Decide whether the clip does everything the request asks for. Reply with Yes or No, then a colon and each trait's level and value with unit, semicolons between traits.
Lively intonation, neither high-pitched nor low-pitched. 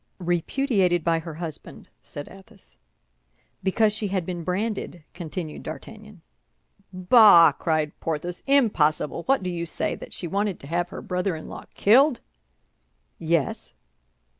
No: average, 4.0 semitones; medium, 180 Hz